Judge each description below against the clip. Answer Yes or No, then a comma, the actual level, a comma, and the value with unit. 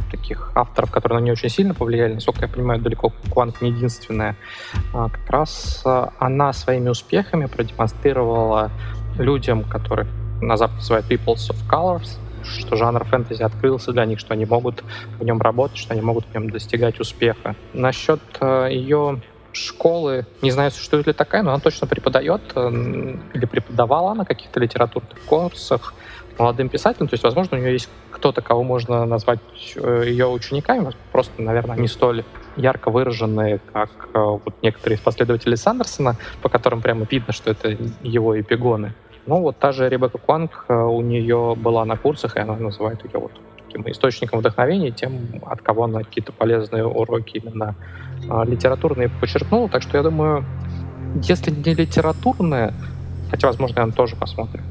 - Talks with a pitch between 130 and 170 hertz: No, low, 120 Hz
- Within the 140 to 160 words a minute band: Yes, average, 155 wpm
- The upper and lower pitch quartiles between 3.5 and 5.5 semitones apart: No, average, 2.7 semitones